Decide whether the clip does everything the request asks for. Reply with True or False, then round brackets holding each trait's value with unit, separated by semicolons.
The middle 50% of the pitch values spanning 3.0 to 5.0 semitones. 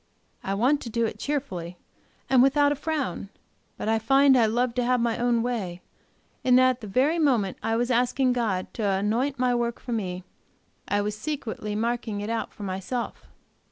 True (3.4 semitones)